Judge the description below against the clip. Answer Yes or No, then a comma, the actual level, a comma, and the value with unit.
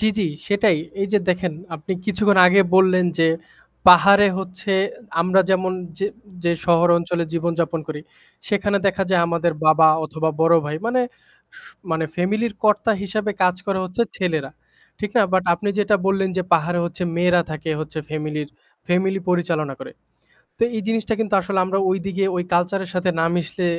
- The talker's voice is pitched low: No, medium, 180 Hz